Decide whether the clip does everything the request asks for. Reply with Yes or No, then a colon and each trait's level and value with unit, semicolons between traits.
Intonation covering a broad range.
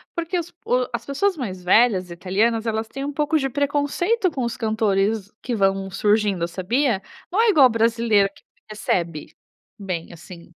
Yes: wide, 6.4 semitones